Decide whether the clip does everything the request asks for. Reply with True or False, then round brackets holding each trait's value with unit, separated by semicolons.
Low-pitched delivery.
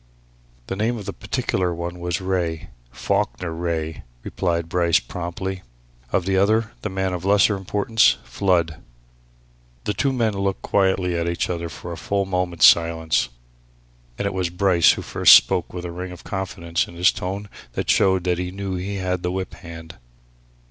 True (90 Hz)